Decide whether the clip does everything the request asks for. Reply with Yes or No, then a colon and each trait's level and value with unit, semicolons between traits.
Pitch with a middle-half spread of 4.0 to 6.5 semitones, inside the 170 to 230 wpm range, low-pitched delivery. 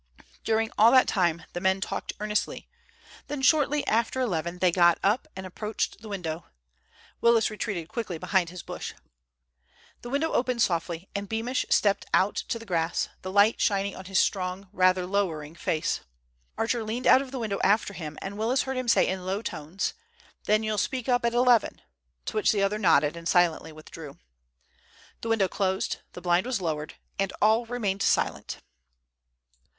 No: average, 4.3 semitones; average, 175 wpm; high, 200 Hz